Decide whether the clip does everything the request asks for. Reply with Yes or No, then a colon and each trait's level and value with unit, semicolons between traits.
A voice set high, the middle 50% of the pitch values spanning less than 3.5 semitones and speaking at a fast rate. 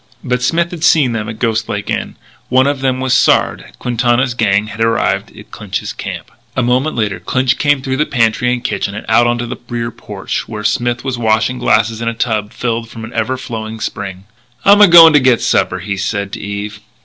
No: low, 120 Hz; average, 2.9 semitones; fast, 215 wpm